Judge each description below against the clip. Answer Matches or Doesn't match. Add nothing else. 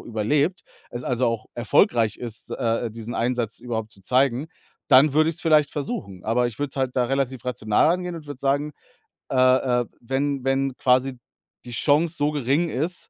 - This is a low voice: Matches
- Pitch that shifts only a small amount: Doesn't match